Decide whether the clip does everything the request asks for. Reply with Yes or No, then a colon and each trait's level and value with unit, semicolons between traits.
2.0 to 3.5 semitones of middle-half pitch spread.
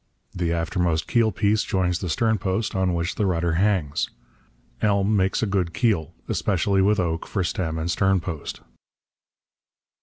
Yes: average, 3.1 semitones